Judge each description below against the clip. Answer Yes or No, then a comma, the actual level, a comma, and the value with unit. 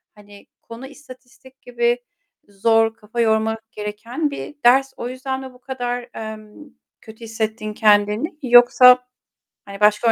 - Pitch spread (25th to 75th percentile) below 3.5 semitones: Yes, average, 2.7 semitones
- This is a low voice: No, high, 235 Hz